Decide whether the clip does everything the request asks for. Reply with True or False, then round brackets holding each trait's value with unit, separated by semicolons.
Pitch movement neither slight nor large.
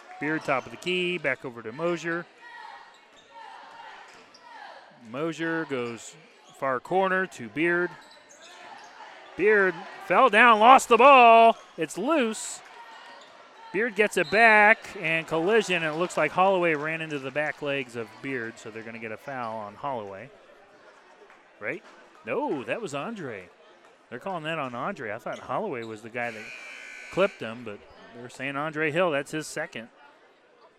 False (8.4 semitones)